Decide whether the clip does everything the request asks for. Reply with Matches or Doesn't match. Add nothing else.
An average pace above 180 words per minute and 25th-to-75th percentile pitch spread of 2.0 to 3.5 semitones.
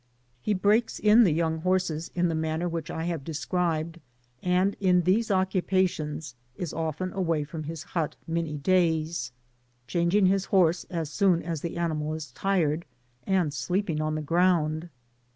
Doesn't match